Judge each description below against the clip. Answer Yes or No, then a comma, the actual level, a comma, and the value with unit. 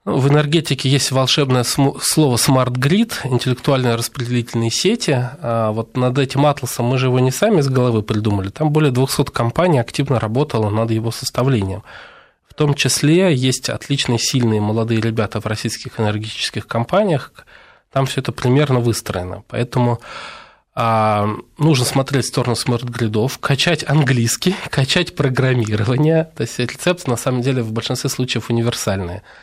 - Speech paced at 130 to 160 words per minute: Yes, average, 140 wpm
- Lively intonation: No, average, 3.3 semitones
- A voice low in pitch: Yes, low, 125 Hz